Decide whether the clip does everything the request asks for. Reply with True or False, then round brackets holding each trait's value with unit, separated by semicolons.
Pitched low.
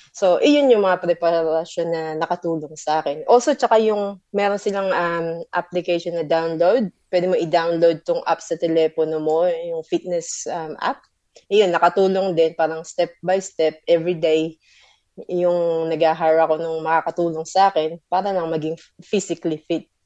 False (170 Hz)